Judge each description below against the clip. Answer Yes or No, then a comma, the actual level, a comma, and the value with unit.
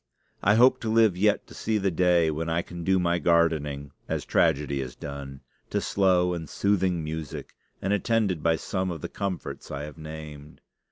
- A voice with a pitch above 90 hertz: No, very low, 85 Hz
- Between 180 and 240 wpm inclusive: Yes, average, 185 wpm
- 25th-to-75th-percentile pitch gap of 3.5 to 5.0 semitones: Yes, average, 3.8 semitones